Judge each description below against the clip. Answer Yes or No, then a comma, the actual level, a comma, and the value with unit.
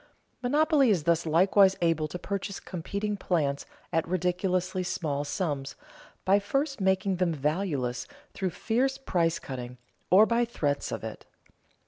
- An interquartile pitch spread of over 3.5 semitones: Yes, average, 4.1 semitones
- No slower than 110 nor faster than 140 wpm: Yes, slow, 135 wpm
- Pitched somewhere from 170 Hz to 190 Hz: Yes, medium, 185 Hz